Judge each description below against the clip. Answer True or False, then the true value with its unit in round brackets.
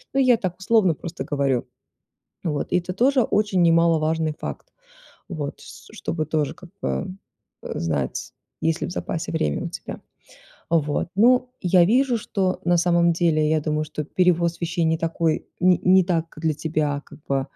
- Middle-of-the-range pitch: True (170 Hz)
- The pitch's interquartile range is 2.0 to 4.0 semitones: True (3.0 semitones)